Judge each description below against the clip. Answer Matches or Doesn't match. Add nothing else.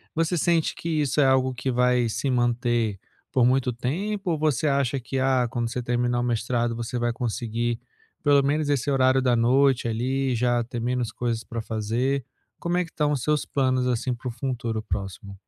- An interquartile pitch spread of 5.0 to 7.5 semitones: Doesn't match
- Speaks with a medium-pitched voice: Doesn't match